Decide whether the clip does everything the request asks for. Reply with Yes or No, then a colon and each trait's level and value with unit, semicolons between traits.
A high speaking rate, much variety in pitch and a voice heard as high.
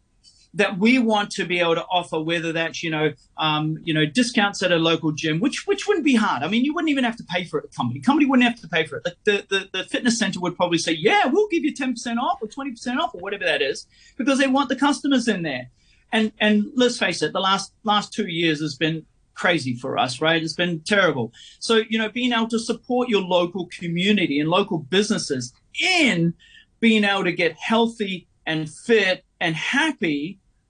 Yes: fast, 230 wpm; wide, 6.6 semitones; high, 200 Hz